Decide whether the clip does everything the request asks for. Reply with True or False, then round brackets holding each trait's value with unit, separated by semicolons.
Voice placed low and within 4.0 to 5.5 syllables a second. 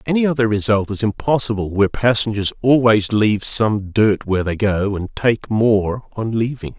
True (110 Hz; 4.9 syllables/s)